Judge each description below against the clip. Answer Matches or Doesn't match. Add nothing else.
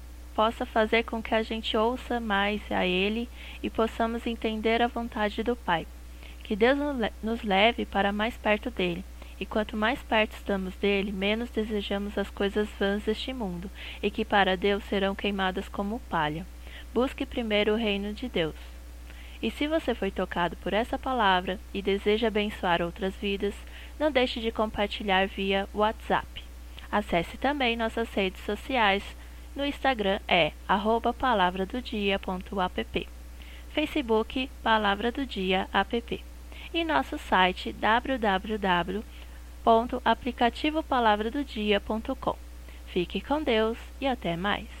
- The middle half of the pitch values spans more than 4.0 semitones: Doesn't match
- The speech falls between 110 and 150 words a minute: Matches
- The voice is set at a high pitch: Matches